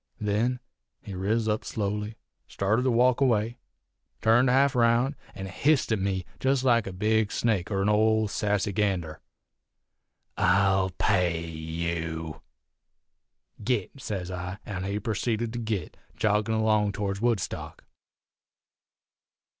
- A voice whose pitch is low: Yes, low, 105 Hz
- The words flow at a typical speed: No, slow, 125 wpm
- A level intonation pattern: No, average, 3.3 semitones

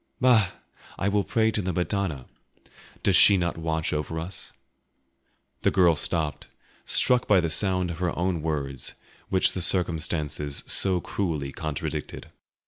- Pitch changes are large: No, average, 3.6 semitones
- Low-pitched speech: Yes, very low, 85 Hz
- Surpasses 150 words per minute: No, average, 140 wpm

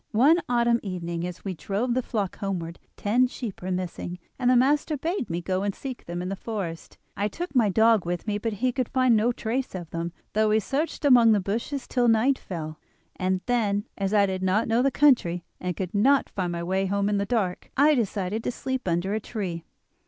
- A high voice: Yes, high, 210 Hz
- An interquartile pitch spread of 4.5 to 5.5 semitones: Yes, average, 4.9 semitones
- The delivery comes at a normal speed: No, fast, 220 wpm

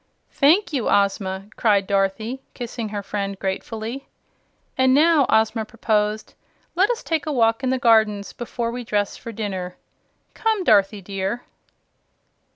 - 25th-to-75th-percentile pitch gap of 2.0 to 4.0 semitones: No, average, 4.4 semitones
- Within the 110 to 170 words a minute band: Yes, average, 140 wpm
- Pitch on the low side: No, high, 220 Hz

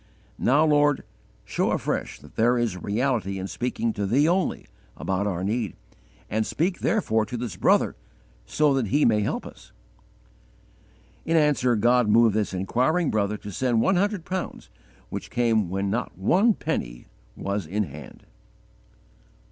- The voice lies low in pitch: Yes, low, 115 Hz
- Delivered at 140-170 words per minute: Yes, average, 150 wpm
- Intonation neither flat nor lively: No, wide, 6.3 semitones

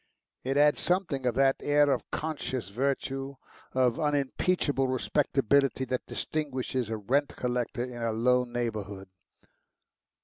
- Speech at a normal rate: No, slow, 125 wpm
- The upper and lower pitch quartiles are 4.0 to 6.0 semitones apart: No, average, 2.7 semitones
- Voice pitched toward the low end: Yes, low, 130 Hz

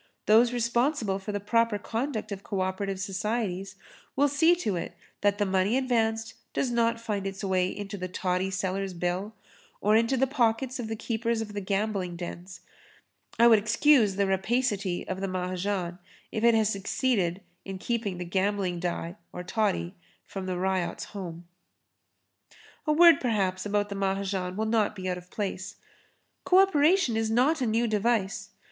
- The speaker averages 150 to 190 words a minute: Yes, average, 165 wpm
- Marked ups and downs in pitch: No, average, 3.5 semitones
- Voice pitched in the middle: No, high, 205 Hz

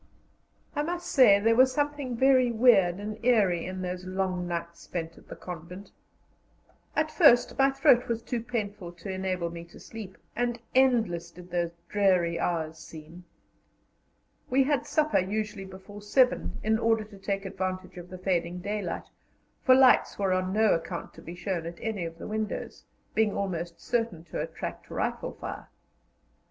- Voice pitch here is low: No, high, 195 Hz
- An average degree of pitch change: Yes, average, 4.8 semitones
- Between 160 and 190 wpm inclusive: Yes, average, 165 wpm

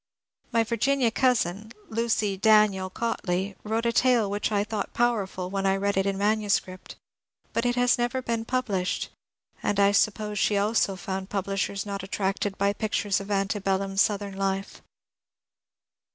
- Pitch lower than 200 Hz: No, high, 205 Hz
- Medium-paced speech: Yes, average, 155 wpm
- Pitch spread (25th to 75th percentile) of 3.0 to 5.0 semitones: No, narrow, 2.4 semitones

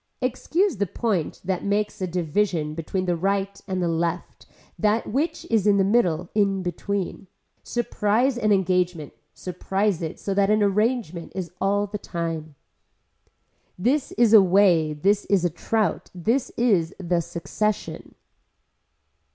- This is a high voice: Yes, high, 195 Hz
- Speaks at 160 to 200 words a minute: No, average, 140 wpm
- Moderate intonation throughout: Yes, average, 3.3 semitones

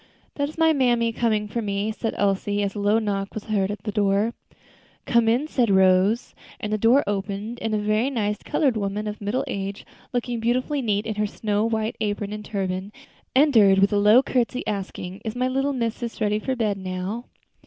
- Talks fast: No, average, 195 wpm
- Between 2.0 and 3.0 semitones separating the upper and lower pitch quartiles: Yes, average, 2.7 semitones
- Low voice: No, high, 215 Hz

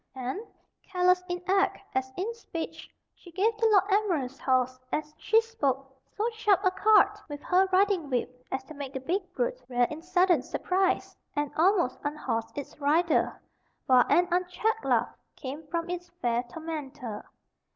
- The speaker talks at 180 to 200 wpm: No, average, 160 wpm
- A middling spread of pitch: No, wide, 6.3 semitones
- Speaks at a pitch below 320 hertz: No, very high, 340 Hz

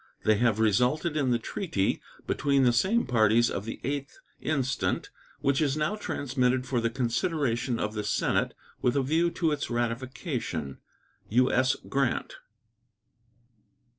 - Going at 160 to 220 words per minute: No, slow, 135 wpm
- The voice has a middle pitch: No, low, 130 Hz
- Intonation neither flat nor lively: Yes, average, 3.6 semitones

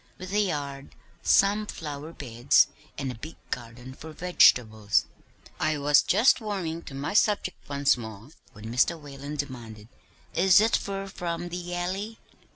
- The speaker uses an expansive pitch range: Yes, wide, 6.0 semitones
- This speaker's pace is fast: No, average, 150 wpm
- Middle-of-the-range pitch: Yes, medium, 150 Hz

